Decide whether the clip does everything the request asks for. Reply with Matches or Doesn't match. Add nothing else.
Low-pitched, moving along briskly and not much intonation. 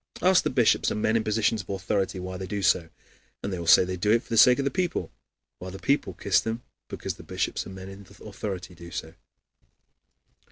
Doesn't match